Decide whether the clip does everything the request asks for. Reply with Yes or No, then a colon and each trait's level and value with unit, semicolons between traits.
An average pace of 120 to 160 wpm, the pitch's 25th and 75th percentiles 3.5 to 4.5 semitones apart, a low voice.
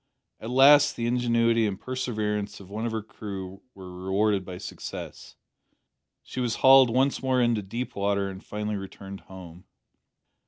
Yes: average, 155 wpm; average, 3.8 semitones; low, 105 Hz